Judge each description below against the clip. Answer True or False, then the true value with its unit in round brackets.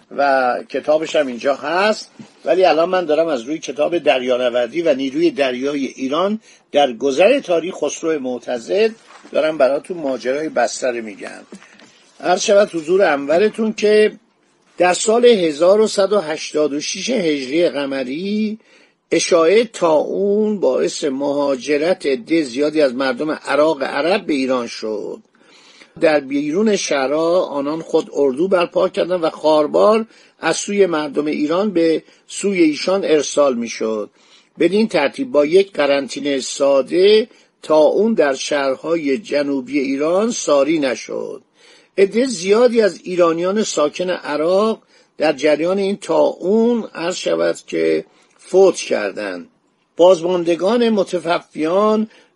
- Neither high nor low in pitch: True (175 Hz)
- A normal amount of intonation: False (6.8 semitones)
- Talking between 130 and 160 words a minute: False (120 wpm)